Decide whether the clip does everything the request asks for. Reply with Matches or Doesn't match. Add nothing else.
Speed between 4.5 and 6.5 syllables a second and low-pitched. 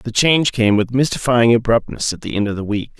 Matches